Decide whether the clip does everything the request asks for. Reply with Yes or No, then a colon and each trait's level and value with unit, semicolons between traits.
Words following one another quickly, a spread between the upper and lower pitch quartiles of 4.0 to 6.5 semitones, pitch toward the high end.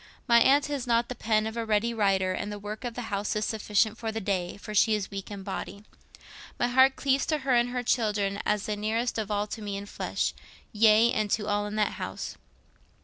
No: fast, 235 wpm; narrow, 2.4 semitones; high, 215 Hz